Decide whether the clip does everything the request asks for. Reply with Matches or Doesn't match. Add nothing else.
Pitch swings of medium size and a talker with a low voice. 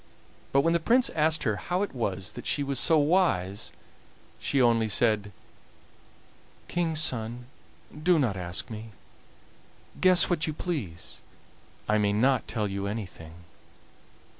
Doesn't match